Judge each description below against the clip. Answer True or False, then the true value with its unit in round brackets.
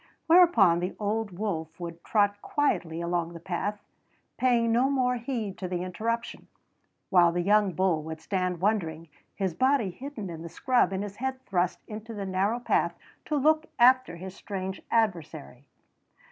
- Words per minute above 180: False (160 wpm)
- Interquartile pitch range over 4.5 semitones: True (5.0 semitones)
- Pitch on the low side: False (195 Hz)